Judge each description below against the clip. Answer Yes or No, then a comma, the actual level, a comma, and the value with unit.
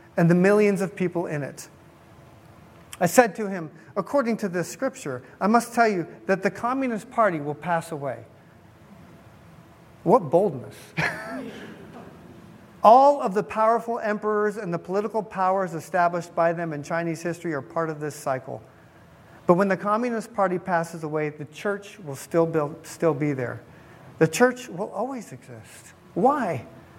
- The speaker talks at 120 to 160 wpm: Yes, average, 150 wpm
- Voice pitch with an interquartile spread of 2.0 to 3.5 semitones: No, average, 4.7 semitones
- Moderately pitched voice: Yes, medium, 180 Hz